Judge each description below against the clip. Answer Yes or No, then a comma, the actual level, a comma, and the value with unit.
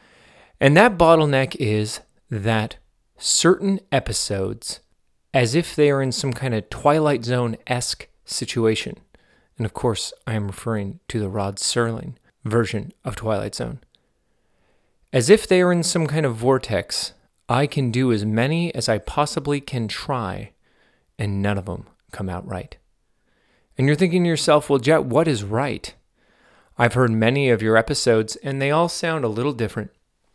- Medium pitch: No, low, 125 Hz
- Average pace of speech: Yes, average, 160 wpm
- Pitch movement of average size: Yes, average, 5.0 semitones